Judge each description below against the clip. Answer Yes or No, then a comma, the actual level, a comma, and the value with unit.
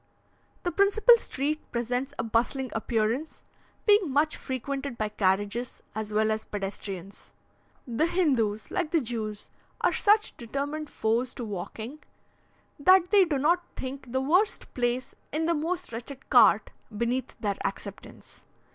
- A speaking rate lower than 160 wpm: Yes, average, 140 wpm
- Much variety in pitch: Yes, wide, 5.9 semitones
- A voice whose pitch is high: Yes, very high, 260 Hz